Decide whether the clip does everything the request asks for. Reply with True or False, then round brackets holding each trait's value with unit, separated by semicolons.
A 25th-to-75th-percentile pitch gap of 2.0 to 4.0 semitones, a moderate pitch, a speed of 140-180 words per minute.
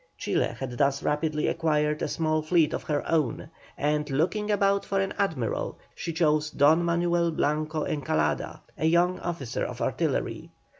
True (2.5 semitones; 155 Hz; 155 wpm)